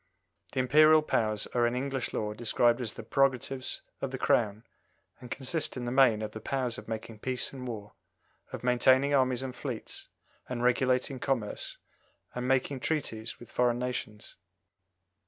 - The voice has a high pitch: No, low, 125 Hz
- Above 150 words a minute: Yes, average, 160 wpm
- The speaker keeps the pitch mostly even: Yes, narrow, 2.1 semitones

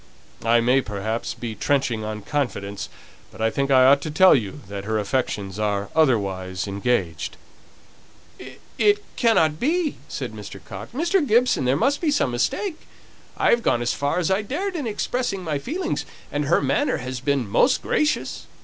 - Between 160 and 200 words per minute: Yes, average, 170 wpm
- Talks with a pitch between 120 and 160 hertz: Yes, medium, 140 Hz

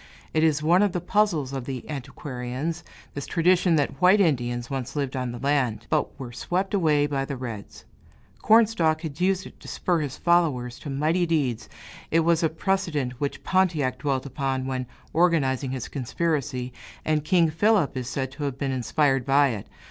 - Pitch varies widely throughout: No, average, 4.3 semitones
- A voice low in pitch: No, medium, 145 Hz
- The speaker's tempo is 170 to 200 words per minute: Yes, average, 180 wpm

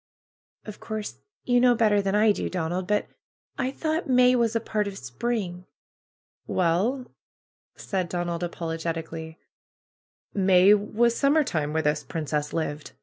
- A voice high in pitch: Yes, high, 195 Hz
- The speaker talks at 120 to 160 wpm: Yes, average, 145 wpm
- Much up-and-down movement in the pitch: Yes, wide, 5.9 semitones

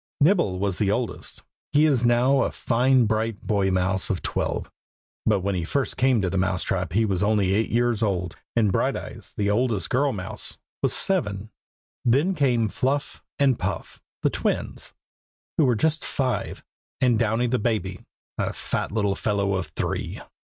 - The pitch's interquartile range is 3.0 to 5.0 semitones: Yes, average, 4.5 semitones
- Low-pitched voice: Yes, low, 110 Hz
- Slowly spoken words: No, average, 170 wpm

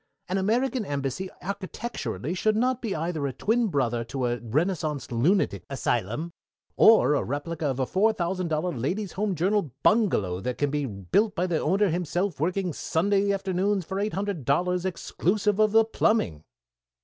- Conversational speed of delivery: Yes, average, 165 wpm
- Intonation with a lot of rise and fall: Yes, wide, 6.1 semitones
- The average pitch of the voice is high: No, medium, 180 Hz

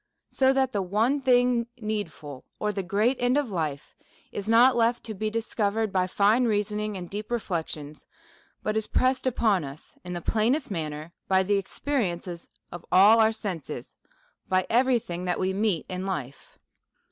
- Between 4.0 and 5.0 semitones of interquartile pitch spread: Yes, average, 4.5 semitones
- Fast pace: No, average, 170 wpm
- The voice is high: Yes, high, 210 Hz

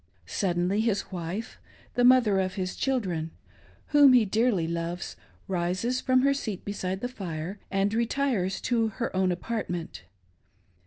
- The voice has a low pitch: No, high, 200 Hz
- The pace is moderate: Yes, average, 150 wpm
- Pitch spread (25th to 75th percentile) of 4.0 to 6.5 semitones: Yes, average, 5.0 semitones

